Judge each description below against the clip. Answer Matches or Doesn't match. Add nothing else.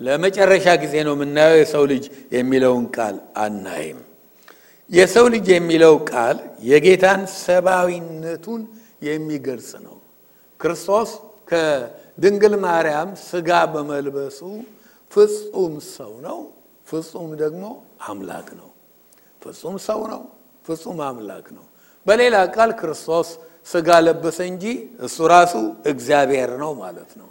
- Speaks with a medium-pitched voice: Matches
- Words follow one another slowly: Matches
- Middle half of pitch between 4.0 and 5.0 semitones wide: Matches